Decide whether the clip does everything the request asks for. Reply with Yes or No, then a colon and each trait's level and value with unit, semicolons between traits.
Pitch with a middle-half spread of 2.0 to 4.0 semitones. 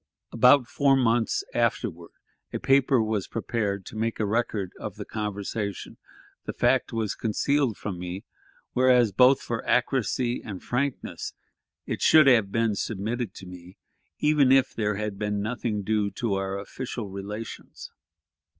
Yes: average, 3.6 semitones